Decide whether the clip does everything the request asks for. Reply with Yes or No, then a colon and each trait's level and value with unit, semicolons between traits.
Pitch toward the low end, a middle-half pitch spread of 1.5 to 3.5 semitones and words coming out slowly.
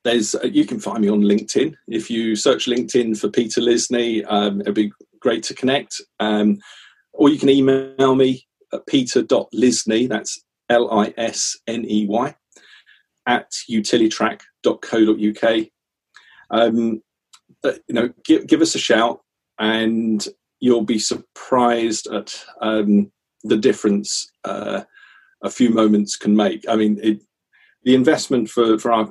Yes: low, 115 Hz; average, 2.8 semitones; slow, 130 wpm